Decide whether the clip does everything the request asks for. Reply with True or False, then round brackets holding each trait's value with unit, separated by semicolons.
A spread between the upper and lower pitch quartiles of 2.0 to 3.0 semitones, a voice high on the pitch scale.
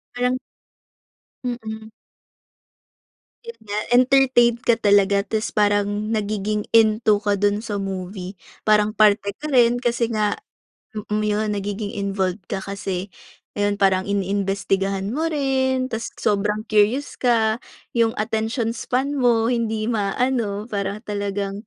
True (2.6 semitones; 215 Hz)